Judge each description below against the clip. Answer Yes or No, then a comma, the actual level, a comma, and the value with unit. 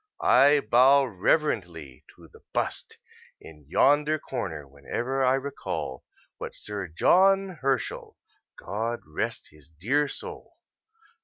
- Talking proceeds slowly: Yes, slow, 110 wpm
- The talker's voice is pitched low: Yes, low, 120 Hz